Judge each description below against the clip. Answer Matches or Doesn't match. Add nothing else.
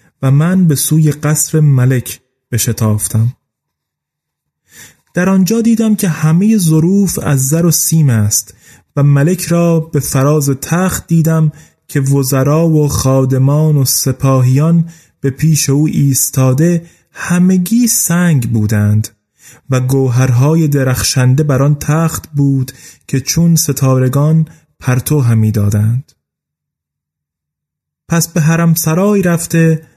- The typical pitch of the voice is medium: Matches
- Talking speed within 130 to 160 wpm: Doesn't match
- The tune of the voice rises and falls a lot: Doesn't match